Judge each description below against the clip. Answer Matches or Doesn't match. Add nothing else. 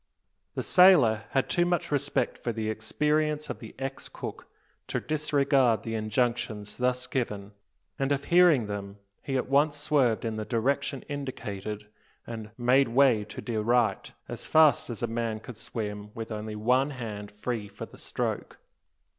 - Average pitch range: Matches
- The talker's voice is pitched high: Doesn't match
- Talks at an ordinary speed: Matches